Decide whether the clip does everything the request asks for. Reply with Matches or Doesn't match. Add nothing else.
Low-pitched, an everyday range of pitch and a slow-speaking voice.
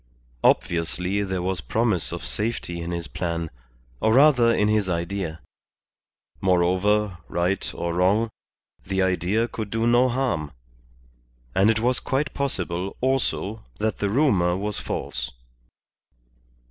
Matches